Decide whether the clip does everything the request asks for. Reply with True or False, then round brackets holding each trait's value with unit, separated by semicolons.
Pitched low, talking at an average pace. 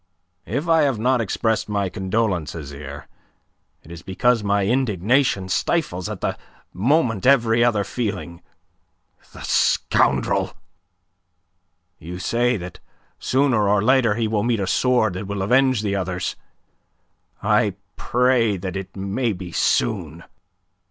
False (105 Hz; 130 wpm)